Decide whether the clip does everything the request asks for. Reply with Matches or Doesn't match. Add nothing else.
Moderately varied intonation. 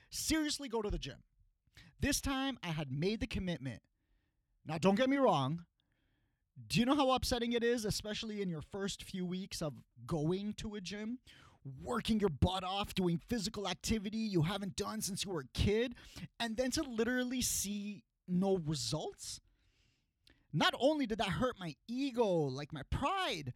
Doesn't match